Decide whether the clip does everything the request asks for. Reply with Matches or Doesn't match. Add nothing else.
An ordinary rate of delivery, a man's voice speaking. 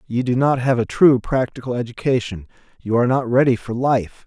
Matches